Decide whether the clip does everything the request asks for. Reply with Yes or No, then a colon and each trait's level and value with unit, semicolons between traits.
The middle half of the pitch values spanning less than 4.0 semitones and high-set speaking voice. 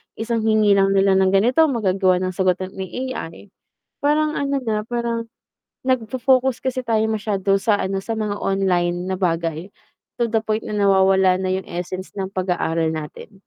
Yes: average, 3.5 semitones; high, 195 Hz